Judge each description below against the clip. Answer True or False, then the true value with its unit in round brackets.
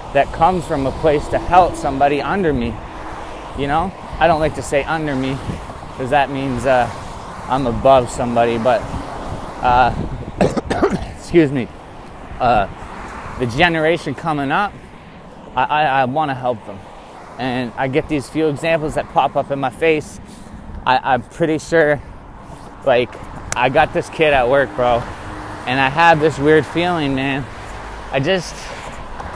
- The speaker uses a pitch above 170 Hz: False (135 Hz)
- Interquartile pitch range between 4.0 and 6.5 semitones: True (4.7 semitones)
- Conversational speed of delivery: True (155 wpm)